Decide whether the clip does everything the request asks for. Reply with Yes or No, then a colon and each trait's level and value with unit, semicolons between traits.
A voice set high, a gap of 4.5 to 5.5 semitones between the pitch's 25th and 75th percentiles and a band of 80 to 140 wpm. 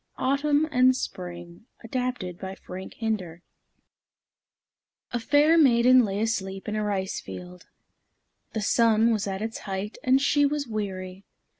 Yes: high, 215 Hz; average, 4.9 semitones; slow, 135 wpm